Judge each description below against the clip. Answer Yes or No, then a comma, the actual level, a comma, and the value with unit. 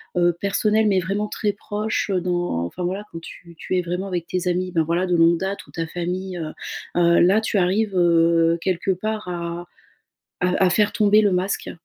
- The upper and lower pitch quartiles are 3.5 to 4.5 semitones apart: No, narrow, 2.6 semitones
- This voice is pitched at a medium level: Yes, medium, 180 Hz